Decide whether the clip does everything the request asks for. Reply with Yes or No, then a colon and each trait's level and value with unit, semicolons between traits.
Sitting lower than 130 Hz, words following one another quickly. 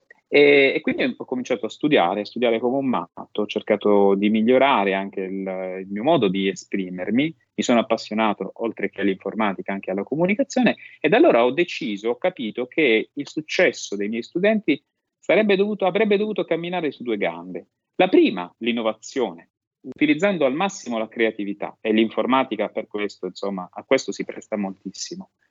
No: low, 115 Hz; average, 160 wpm